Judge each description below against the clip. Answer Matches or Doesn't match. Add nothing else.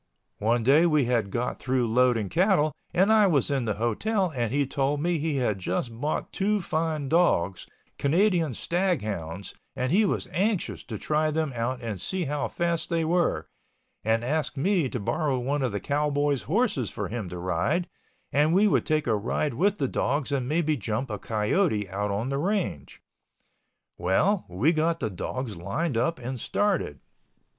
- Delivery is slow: Doesn't match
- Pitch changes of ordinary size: Doesn't match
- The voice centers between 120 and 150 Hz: Matches